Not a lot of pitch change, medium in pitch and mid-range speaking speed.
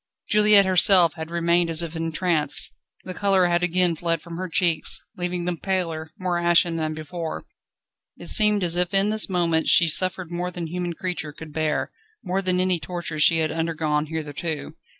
Yes: narrow, 2.1 semitones; medium, 175 Hz; average, 180 wpm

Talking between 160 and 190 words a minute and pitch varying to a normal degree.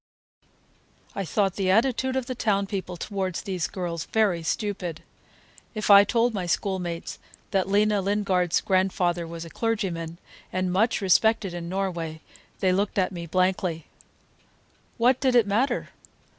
No: average, 145 wpm; average, 3.1 semitones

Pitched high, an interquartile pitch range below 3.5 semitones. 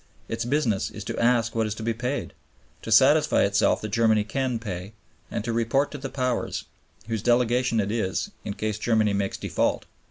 No: low, 115 Hz; narrow, 2.4 semitones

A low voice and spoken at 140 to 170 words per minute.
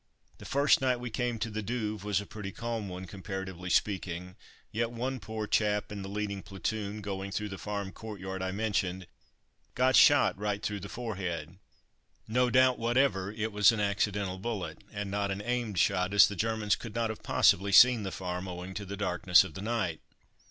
No: low, 105 Hz; average, 195 wpm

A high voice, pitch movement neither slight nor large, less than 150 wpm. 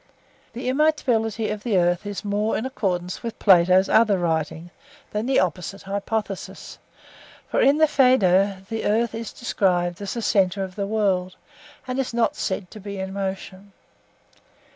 No: high, 200 Hz; average, 3.3 semitones; average, 165 wpm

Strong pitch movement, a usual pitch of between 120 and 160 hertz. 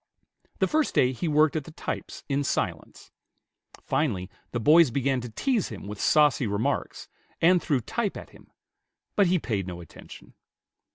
Yes: wide, 6.7 semitones; medium, 140 Hz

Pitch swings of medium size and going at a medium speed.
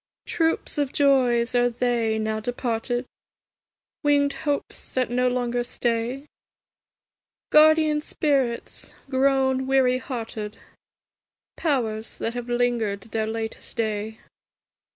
No: average, 3.0 semitones; slow, 100 wpm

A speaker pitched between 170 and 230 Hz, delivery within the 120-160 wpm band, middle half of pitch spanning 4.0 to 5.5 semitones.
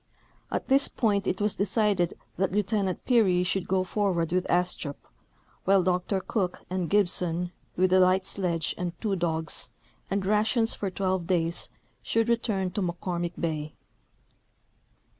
No: medium, 185 Hz; average, 140 wpm; narrow, 2.5 semitones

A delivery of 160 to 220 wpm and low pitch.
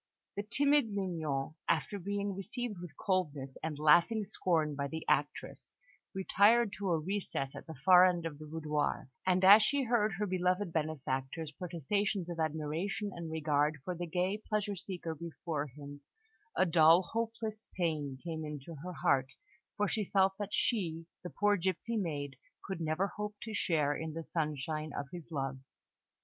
No: average, 165 wpm; medium, 170 Hz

